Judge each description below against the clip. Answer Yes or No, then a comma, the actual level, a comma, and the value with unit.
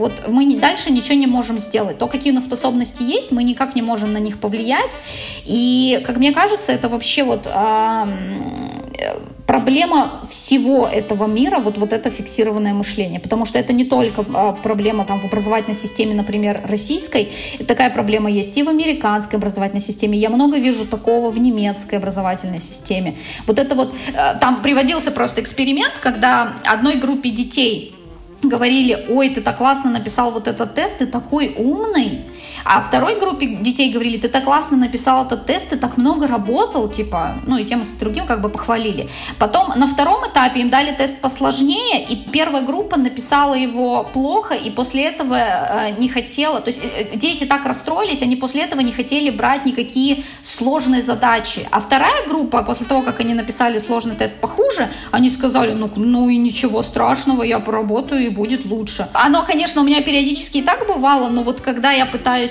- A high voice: Yes, very high, 250 Hz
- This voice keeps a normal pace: No, fast, 175 wpm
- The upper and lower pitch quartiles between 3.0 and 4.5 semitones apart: Yes, average, 3.5 semitones